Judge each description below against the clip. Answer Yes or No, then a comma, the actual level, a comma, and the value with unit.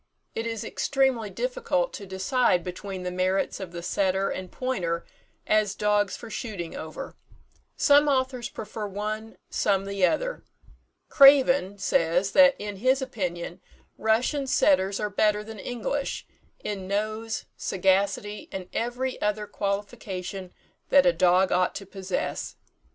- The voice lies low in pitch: No, high, 205 Hz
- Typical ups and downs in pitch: Yes, average, 4.4 semitones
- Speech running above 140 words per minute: No, slow, 135 wpm